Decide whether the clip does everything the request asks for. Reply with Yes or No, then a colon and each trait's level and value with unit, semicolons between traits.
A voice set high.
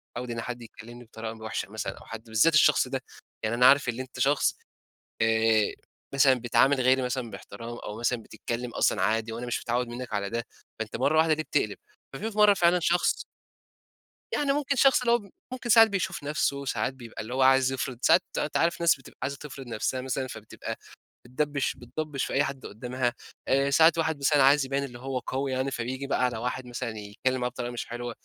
No: low, 130 Hz